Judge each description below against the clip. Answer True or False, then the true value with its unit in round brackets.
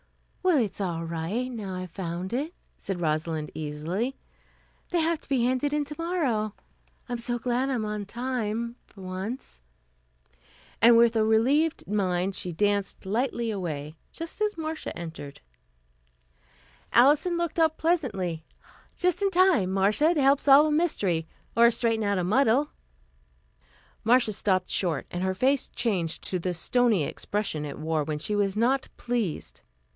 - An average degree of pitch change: False (6.8 semitones)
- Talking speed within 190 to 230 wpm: False (150 wpm)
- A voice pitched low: False (220 Hz)